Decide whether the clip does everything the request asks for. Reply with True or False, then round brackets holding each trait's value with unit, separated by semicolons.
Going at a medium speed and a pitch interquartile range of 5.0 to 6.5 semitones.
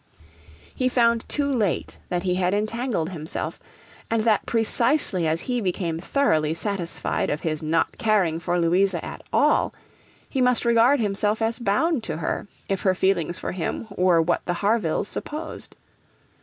True (155 wpm; 5.3 semitones)